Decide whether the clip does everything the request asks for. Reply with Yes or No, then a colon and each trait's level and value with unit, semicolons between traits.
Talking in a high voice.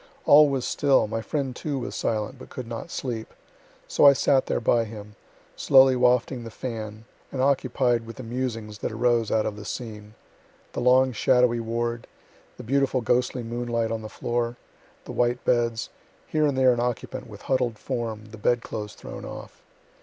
No: low, 120 Hz